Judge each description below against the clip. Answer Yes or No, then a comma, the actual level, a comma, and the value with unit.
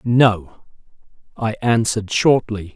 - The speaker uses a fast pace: No, slow, 85 wpm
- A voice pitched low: Yes, low, 110 Hz